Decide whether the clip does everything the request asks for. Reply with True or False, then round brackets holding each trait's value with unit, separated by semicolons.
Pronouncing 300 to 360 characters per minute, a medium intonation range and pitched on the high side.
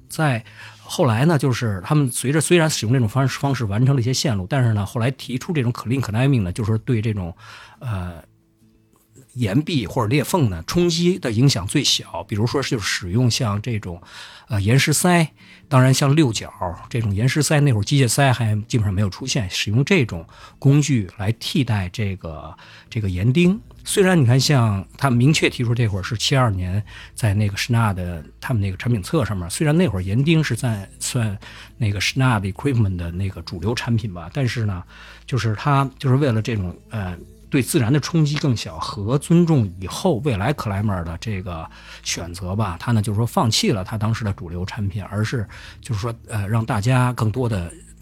False (320 characters per minute; 4.8 semitones; 115 Hz)